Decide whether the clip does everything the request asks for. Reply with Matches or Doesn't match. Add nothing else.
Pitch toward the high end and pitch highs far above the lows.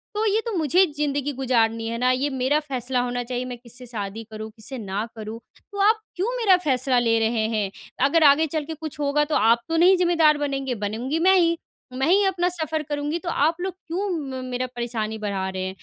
Matches